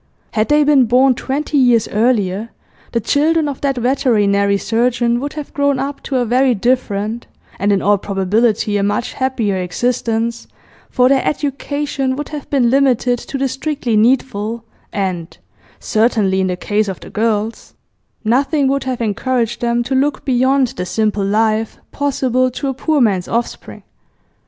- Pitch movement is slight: No, average, 4.1 semitones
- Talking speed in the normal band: Yes, average, 160 wpm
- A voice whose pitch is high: Yes, high, 240 Hz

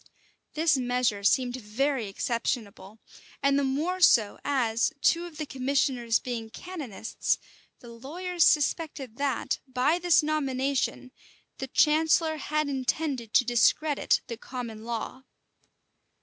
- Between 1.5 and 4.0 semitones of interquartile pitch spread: No, average, 4.4 semitones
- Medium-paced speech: No, slow, 120 wpm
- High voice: Yes, very high, 265 Hz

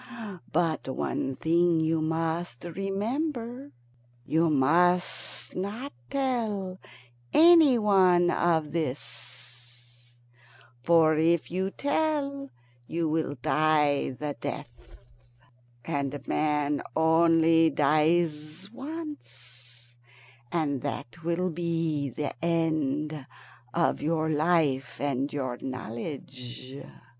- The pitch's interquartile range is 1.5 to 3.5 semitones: No, average, 4.0 semitones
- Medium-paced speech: No, slow, 90 wpm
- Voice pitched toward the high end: No, medium, 160 Hz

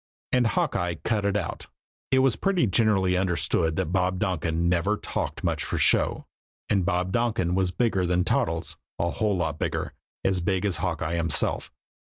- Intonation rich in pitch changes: No, average, 3.2 semitones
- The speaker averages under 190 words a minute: Yes, average, 170 wpm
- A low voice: Yes, very low, 90 Hz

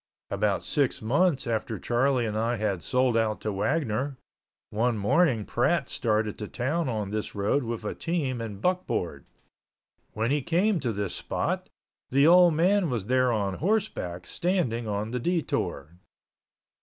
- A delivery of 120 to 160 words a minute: Yes, average, 155 wpm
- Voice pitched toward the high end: No, low, 120 Hz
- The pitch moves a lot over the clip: Yes, wide, 5.9 semitones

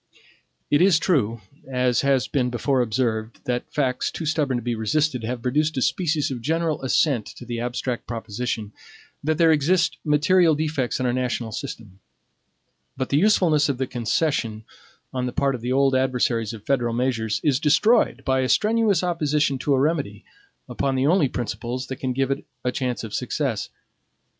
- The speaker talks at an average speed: Yes, average, 175 wpm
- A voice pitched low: Yes, low, 130 Hz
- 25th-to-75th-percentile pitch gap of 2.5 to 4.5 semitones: Yes, average, 3.8 semitones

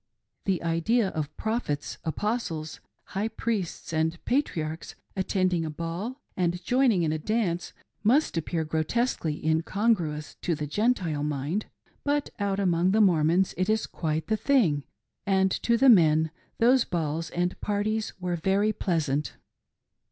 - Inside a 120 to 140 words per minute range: Yes, slow, 135 wpm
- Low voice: No, medium, 180 Hz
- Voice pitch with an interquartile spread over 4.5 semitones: Yes, average, 5.3 semitones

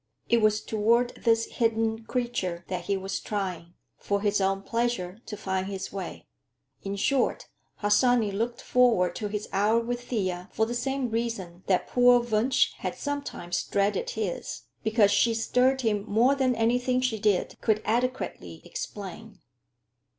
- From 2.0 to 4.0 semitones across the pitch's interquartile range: Yes, average, 3.5 semitones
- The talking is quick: No, average, 150 wpm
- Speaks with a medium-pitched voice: No, high, 220 Hz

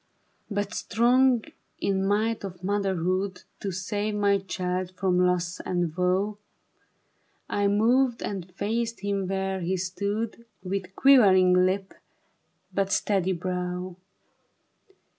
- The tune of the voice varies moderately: No, narrow, 2.0 semitones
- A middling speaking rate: No, slow, 110 wpm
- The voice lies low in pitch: No, high, 195 Hz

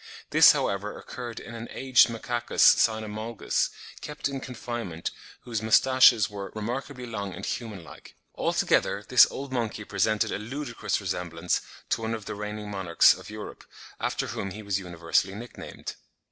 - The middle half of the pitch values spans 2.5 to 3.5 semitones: Yes, average, 3.1 semitones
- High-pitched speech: No, low, 110 Hz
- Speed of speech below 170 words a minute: Yes, average, 155 wpm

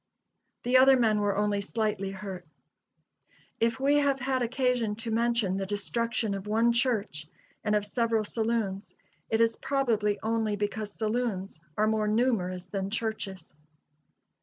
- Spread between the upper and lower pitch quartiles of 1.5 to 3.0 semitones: Yes, narrow, 2.5 semitones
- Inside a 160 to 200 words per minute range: No, average, 140 wpm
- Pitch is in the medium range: No, high, 220 Hz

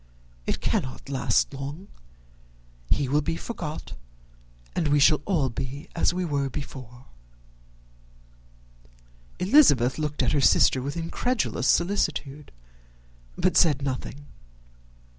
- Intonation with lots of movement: No, average, 3.7 semitones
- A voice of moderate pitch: Yes, medium, 145 Hz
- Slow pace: Yes, slow, 110 wpm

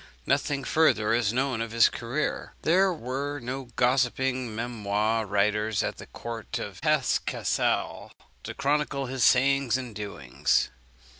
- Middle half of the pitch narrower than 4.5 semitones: Yes, average, 3.7 semitones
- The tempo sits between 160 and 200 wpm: No, slow, 135 wpm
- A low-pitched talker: Yes, low, 125 Hz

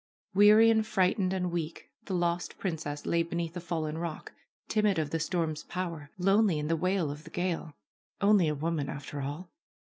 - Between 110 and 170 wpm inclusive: No, average, 180 wpm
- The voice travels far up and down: No, average, 3.2 semitones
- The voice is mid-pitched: Yes, medium, 170 Hz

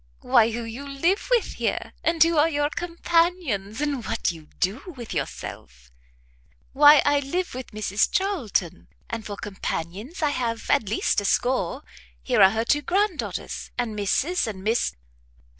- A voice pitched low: No, very high, 250 Hz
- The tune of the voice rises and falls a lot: Yes, wide, 7.0 semitones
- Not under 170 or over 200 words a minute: No, average, 160 wpm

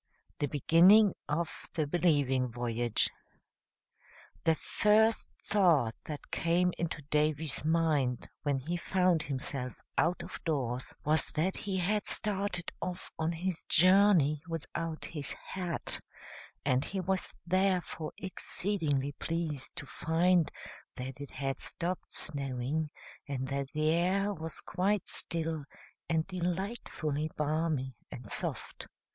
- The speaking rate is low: Yes, slow, 120 wpm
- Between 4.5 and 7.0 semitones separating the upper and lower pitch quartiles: No, average, 4.1 semitones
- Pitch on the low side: No, medium, 160 Hz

